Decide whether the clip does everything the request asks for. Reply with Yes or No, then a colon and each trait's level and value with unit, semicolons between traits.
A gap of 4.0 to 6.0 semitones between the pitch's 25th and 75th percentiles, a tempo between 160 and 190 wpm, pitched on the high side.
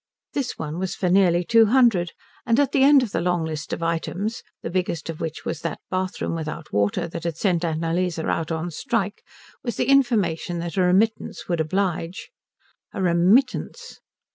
No: average, 4.6 semitones; average, 180 wpm; medium, 180 Hz